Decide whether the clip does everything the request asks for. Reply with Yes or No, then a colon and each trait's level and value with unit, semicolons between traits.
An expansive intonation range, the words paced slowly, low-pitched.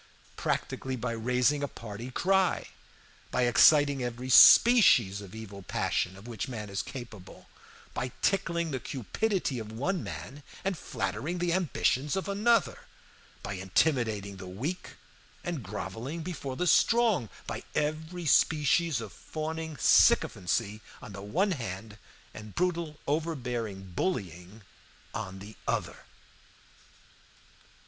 Yes: wide, 7.7 semitones; slow, 125 wpm; low, 130 Hz